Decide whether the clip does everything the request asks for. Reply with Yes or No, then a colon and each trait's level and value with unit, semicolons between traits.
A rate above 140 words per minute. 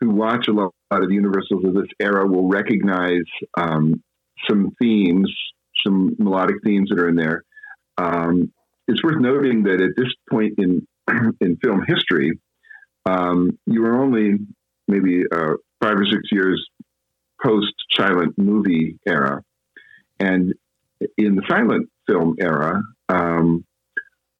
No: slow, 135 wpm